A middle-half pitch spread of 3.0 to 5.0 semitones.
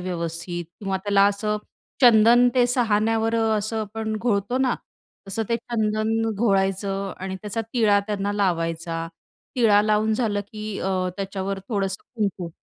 No: narrow, 2.5 semitones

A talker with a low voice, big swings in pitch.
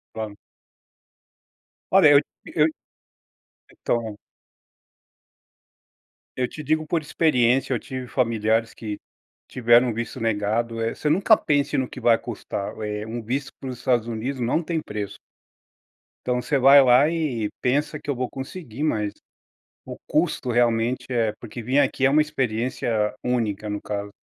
No: low, 125 Hz; average, 3.8 semitones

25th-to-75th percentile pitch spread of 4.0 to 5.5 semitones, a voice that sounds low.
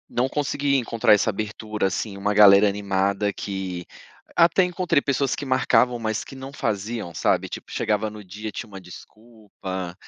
Yes: average, 4.3 semitones; low, 105 Hz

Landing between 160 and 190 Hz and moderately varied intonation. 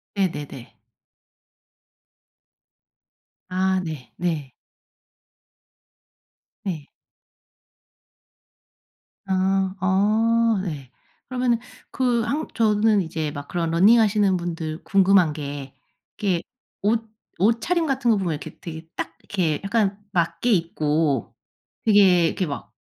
Yes: medium, 185 Hz; average, 4.9 semitones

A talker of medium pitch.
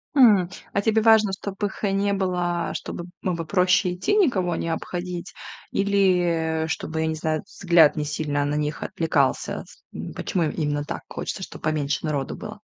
Yes: medium, 175 Hz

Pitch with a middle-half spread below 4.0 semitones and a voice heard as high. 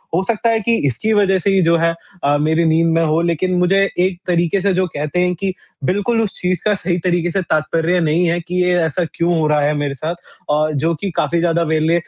No: narrow, 2.5 semitones; medium, 170 Hz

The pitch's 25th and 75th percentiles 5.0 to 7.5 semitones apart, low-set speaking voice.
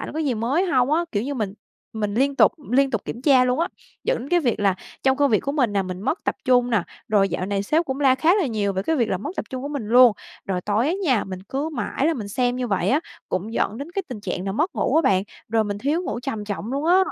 No: wide, 5.6 semitones; very high, 250 Hz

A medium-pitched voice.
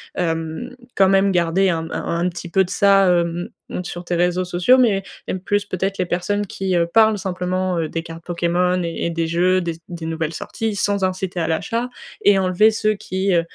Yes: medium, 180 Hz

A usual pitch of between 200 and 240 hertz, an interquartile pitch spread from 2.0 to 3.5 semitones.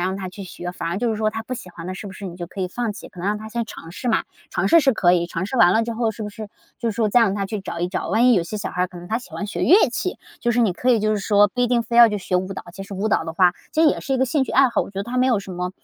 No: high, 210 Hz; average, 4.3 semitones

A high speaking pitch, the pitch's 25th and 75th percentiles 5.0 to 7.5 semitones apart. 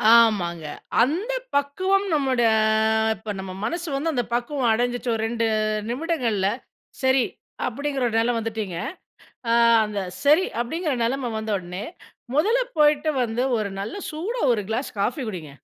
Yes: high, 245 Hz; average, 5.3 semitones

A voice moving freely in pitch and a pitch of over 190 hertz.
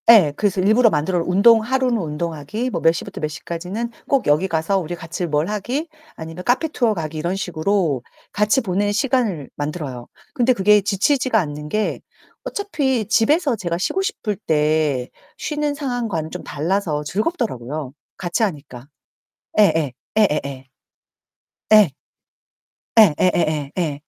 No: wide, 6.7 semitones; medium, 185 Hz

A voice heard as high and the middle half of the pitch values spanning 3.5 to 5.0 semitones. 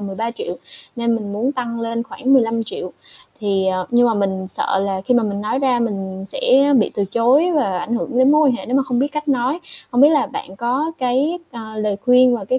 Yes: high, 240 Hz; average, 4.4 semitones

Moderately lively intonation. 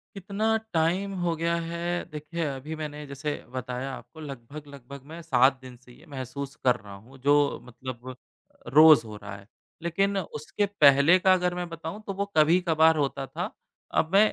Yes: average, 4.3 semitones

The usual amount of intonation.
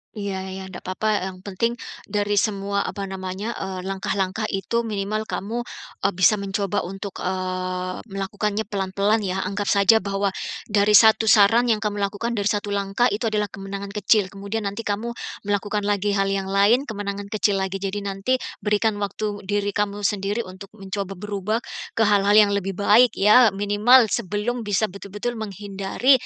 No: narrow, 1.5 semitones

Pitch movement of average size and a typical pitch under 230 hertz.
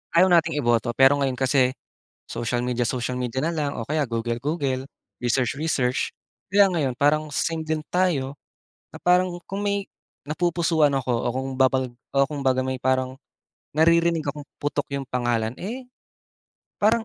Yes: average, 4.5 semitones; medium, 140 Hz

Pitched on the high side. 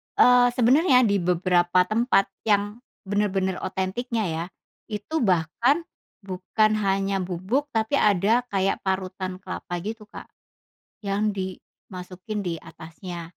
Yes: high, 195 Hz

